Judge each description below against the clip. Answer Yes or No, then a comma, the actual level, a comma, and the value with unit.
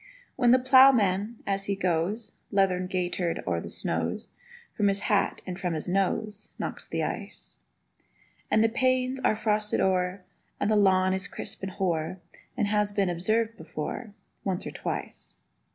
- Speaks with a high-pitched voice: Yes, high, 195 Hz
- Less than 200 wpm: Yes, average, 160 wpm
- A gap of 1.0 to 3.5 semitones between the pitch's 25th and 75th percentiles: Yes, average, 2.9 semitones